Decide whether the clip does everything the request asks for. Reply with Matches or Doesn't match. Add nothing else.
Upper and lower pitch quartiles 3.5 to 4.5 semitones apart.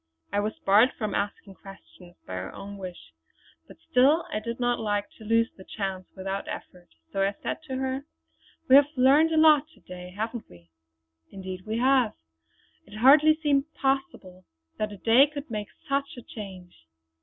Doesn't match